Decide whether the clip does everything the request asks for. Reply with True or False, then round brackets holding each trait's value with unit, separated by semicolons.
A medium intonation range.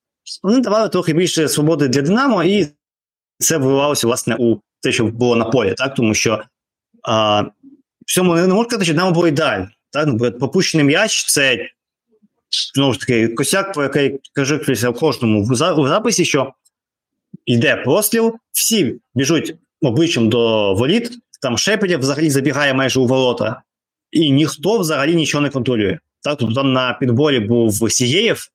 False (6.8 semitones)